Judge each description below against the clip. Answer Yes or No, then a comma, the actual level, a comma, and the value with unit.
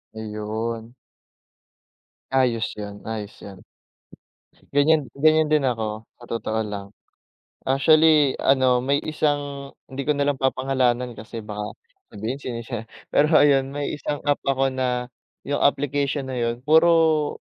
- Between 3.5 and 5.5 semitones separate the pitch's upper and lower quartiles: Yes, average, 3.9 semitones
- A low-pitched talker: Yes, low, 130 Hz